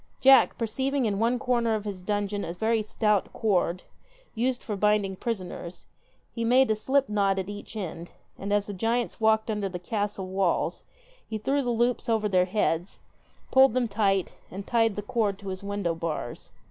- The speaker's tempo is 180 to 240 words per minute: Yes, average, 185 wpm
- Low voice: No, high, 210 Hz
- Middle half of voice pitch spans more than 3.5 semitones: No, average, 3.0 semitones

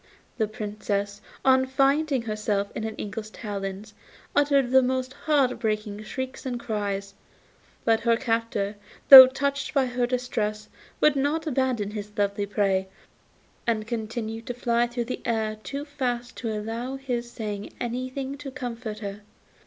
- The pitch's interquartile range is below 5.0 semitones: Yes, average, 3.6 semitones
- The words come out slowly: No, average, 150 wpm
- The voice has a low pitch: No, high, 235 Hz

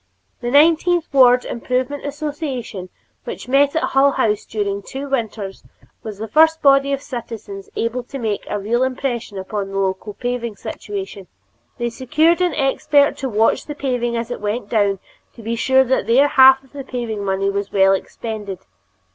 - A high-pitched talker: Yes, high, 245 Hz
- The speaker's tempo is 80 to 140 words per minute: No, average, 170 wpm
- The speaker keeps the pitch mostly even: No, average, 4.8 semitones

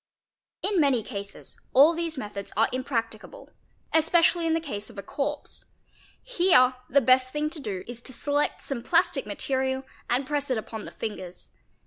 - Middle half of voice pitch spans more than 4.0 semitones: Yes, average, 4.9 semitones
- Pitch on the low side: No, very high, 265 Hz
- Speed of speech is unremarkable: Yes, average, 165 wpm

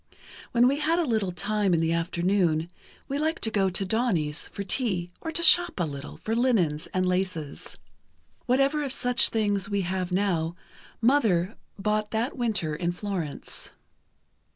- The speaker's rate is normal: Yes, average, 160 wpm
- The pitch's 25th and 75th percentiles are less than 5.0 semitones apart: No, wide, 5.6 semitones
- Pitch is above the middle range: Yes, high, 200 Hz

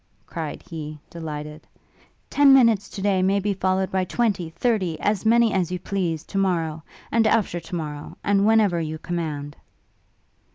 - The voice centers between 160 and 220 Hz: Yes, medium, 185 Hz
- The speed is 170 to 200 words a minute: No, average, 160 wpm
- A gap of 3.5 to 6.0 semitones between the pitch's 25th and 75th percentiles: Yes, average, 4.2 semitones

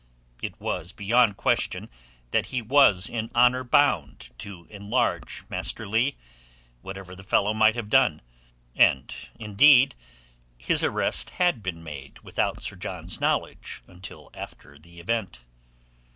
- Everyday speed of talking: No, slow, 130 wpm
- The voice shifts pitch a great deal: Yes, wide, 5.8 semitones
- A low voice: Yes, low, 105 Hz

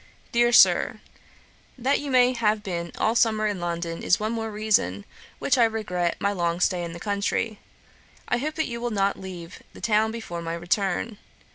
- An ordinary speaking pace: Yes, average, 185 wpm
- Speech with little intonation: No, average, 4.7 semitones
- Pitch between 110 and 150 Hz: No, high, 210 Hz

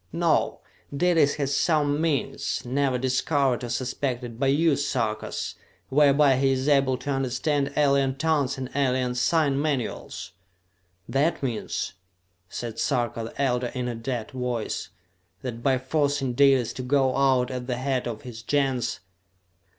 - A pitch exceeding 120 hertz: Yes, low, 135 Hz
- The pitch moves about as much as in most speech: No, narrow, 2.3 semitones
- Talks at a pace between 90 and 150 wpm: Yes, average, 145 wpm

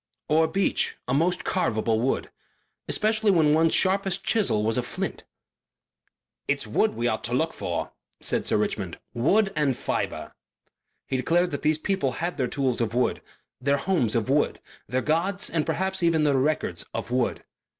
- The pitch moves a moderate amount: No, wide, 6.2 semitones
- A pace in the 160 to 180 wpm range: Yes, average, 165 wpm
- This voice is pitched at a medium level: Yes, medium, 150 Hz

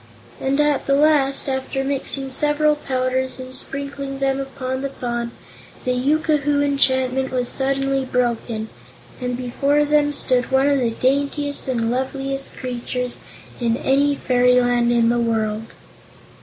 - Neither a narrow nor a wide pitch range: No, narrow, 2.0 semitones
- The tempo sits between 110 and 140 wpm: Yes, slow, 135 wpm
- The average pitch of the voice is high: Yes, very high, 265 Hz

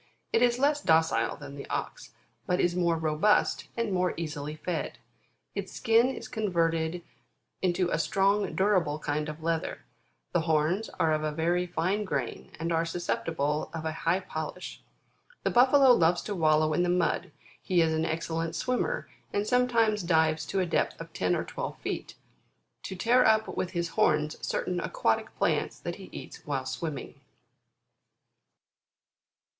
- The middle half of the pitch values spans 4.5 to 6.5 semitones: No, average, 3.8 semitones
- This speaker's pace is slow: No, average, 160 wpm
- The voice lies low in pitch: No, medium, 170 Hz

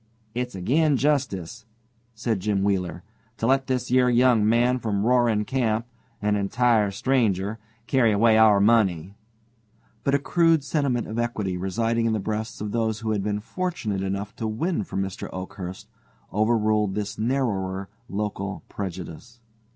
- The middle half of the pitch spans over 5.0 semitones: No, average, 3.7 semitones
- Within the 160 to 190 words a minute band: No, average, 150 wpm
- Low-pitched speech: Yes, low, 110 Hz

